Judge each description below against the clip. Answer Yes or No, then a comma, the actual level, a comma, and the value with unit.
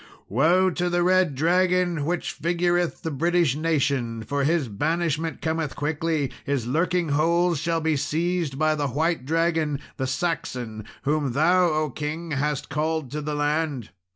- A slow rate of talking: No, average, 150 wpm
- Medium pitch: Yes, medium, 155 Hz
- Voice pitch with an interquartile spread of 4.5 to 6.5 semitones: No, average, 3.1 semitones